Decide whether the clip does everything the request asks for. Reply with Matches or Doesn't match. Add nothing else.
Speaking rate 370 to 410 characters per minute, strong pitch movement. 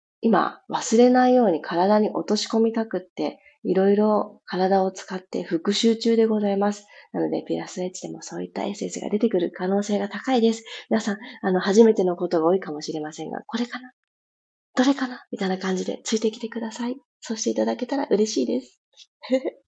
Doesn't match